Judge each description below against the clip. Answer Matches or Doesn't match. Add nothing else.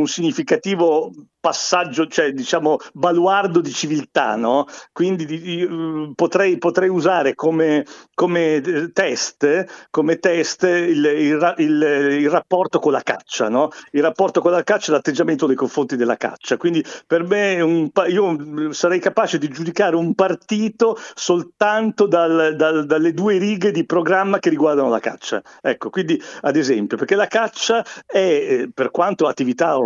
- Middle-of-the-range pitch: Matches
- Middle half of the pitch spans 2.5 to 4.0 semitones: Matches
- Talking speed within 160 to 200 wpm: Doesn't match